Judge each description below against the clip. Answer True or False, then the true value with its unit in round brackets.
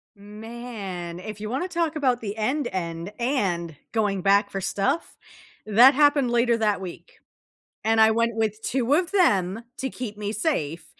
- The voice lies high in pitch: True (220 Hz)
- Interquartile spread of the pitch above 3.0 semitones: True (4.4 semitones)